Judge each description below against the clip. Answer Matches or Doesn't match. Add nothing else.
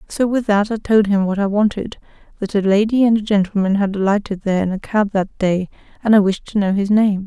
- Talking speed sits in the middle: Doesn't match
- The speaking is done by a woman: Matches